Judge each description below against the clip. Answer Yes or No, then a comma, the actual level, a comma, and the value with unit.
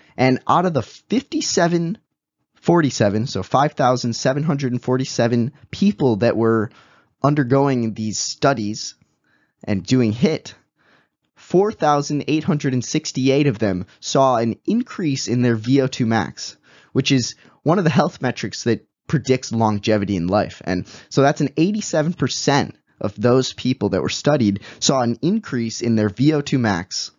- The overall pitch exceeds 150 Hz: No, low, 130 Hz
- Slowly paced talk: Yes, slow, 125 wpm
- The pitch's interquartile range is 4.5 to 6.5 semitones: Yes, average, 4.8 semitones